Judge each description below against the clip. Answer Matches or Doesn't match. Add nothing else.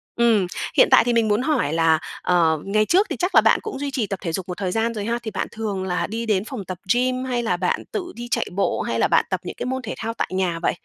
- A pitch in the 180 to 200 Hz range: Doesn't match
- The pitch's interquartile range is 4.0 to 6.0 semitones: Matches